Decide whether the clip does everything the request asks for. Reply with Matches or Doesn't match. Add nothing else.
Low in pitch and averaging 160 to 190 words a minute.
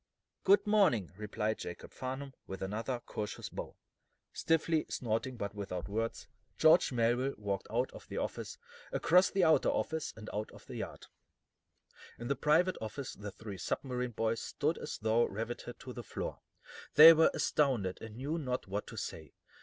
Matches